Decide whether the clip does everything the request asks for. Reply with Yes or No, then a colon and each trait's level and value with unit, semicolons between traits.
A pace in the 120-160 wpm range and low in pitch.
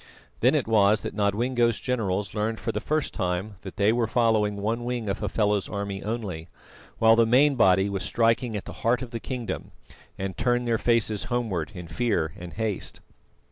No: average, 185 wpm; low, 110 Hz